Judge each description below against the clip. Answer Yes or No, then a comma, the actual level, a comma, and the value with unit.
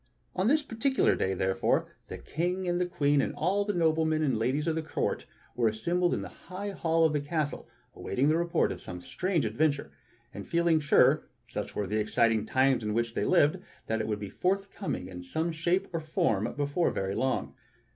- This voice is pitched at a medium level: Yes, medium, 155 Hz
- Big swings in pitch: Yes, wide, 7.2 semitones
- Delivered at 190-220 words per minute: Yes, average, 200 wpm